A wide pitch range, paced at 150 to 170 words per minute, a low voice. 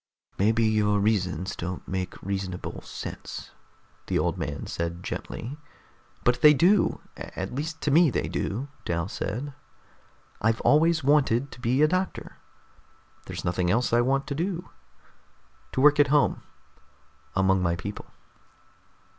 No: wide, 7.4 semitones; average, 140 wpm; low, 115 Hz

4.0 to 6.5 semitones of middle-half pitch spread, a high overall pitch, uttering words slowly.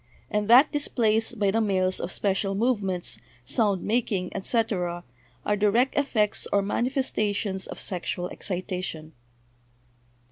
No: average, 3.4 semitones; high, 205 Hz; slow, 120 wpm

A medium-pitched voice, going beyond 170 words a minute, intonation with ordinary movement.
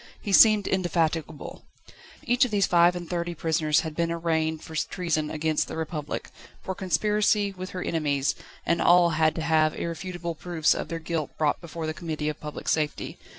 No: medium, 165 Hz; average, 180 wpm; narrow, 2.3 semitones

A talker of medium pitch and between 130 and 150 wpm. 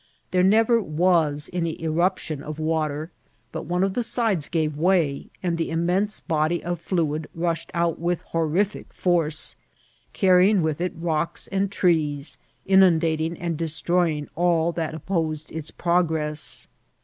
Yes: medium, 165 Hz; average, 145 wpm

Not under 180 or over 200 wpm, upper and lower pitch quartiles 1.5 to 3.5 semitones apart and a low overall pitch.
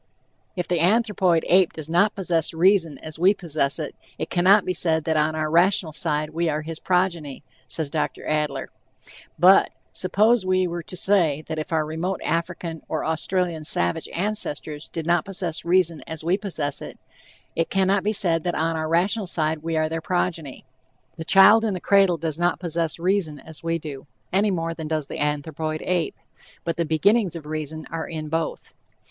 No: average, 190 wpm; average, 2.8 semitones; medium, 165 Hz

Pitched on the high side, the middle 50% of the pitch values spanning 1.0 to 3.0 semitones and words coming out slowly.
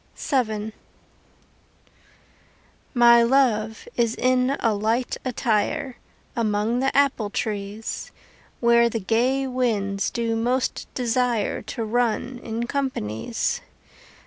Yes: high, 235 Hz; narrow, 2.6 semitones; slow, 95 wpm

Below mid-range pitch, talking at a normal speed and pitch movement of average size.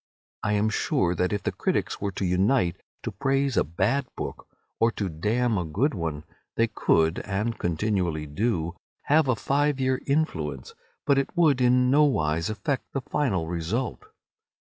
No: low, 110 Hz; average, 170 wpm; wide, 7.7 semitones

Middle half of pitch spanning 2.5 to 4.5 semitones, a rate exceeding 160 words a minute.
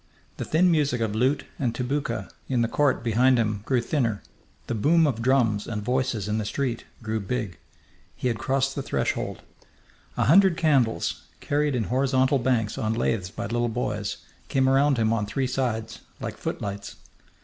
Yes: average, 3.5 semitones; average, 170 wpm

